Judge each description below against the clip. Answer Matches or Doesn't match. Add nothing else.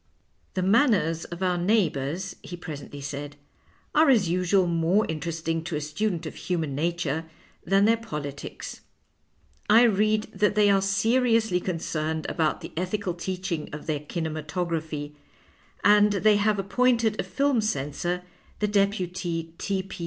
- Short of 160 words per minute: Matches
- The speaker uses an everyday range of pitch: Matches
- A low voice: Doesn't match